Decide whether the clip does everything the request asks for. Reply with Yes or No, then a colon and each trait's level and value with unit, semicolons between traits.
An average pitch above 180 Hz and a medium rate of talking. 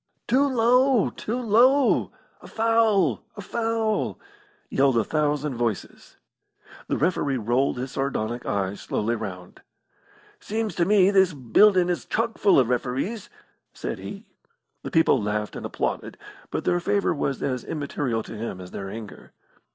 No: medium, 150 Hz; average, 145 wpm